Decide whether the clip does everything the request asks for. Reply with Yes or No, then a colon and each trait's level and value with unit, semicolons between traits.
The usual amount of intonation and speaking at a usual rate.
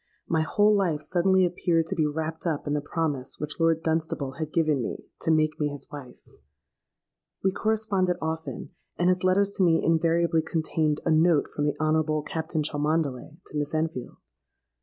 No: narrow, 2.1 semitones; average, 175 wpm